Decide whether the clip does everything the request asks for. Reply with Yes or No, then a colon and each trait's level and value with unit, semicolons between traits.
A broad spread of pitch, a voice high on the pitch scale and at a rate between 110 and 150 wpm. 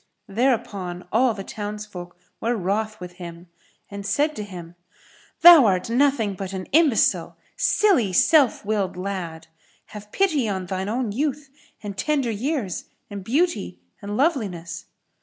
Yes: wide, 5.8 semitones; high, 210 Hz; average, 140 wpm